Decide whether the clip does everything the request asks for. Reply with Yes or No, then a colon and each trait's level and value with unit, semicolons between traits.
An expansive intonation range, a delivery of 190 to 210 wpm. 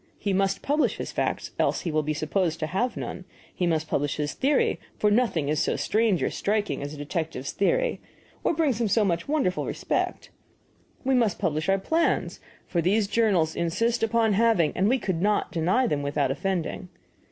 Yes: wide, 6.1 semitones; average, 195 wpm